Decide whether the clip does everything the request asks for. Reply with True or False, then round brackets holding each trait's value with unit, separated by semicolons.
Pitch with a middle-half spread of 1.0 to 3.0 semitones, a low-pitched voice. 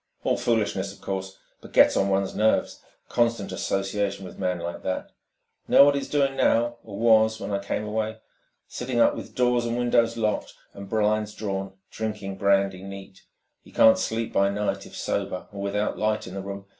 True (2.4 semitones; 105 Hz)